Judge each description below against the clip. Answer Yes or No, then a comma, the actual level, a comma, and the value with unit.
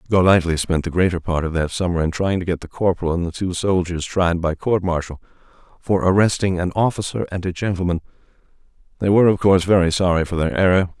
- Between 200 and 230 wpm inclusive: Yes, fast, 205 wpm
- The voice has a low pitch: Yes, very low, 90 Hz